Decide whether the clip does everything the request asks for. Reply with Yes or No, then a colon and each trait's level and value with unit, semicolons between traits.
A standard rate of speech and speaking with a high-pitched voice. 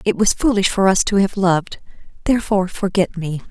Yes: average, 190 wpm; high, 195 Hz